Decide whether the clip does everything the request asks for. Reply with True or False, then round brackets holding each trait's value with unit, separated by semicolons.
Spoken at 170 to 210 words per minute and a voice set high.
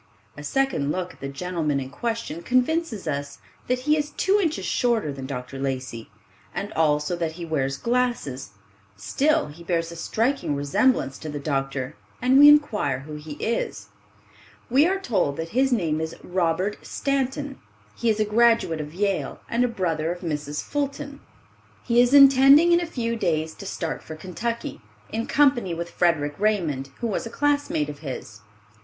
False (175 wpm; 180 Hz)